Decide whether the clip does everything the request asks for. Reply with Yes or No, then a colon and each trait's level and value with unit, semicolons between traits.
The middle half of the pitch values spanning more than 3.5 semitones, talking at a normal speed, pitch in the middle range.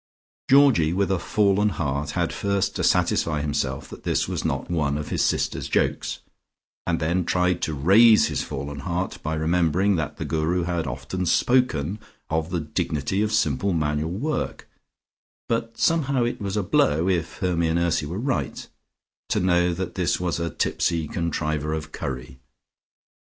No: average, 4.0 semitones; average, 165 wpm; very low, 85 Hz